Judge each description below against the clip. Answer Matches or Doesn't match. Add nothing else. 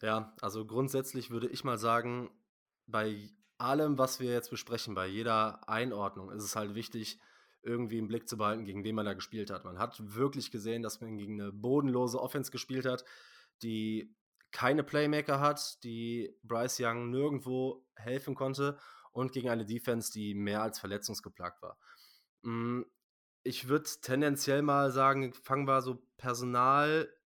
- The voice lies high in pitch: Doesn't match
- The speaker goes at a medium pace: Matches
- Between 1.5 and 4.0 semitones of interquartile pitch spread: Matches